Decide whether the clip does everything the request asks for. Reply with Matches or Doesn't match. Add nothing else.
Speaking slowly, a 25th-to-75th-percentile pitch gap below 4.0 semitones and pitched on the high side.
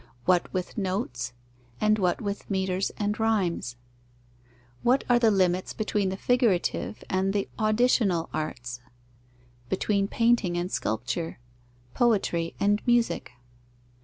Matches